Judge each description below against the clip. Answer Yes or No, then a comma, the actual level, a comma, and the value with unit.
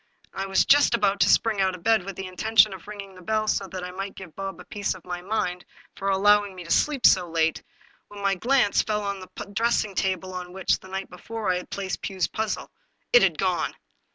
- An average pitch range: No, narrow, 2.3 semitones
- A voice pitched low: No, high, 195 Hz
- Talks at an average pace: No, fast, 235 wpm